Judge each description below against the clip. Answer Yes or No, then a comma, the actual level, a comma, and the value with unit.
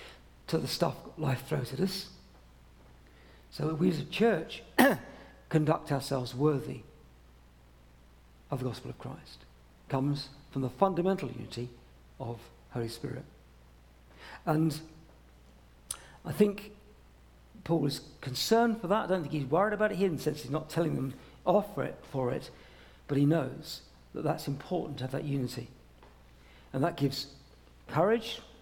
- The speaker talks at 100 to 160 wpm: Yes, average, 145 wpm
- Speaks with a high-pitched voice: No, low, 135 Hz